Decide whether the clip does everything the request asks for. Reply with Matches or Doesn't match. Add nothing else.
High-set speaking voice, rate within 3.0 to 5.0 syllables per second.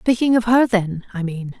Matches